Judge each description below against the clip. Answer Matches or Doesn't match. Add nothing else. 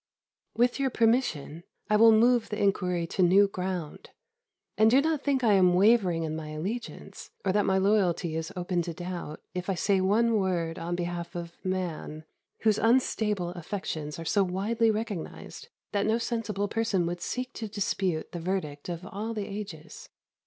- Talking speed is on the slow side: Doesn't match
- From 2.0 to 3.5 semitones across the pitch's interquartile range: Doesn't match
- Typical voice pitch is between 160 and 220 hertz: Matches